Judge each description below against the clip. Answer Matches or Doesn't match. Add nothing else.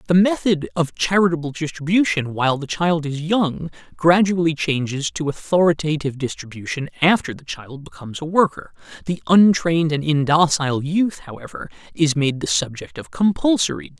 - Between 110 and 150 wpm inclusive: Matches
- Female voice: Doesn't match